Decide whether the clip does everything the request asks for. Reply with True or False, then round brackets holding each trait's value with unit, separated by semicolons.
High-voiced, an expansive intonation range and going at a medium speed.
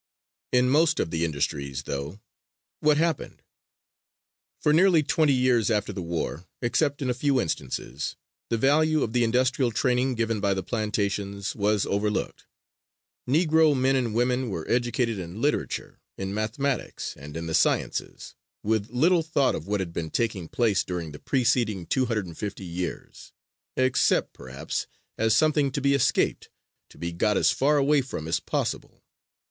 False (115 Hz; 6.0 semitones; 160 wpm)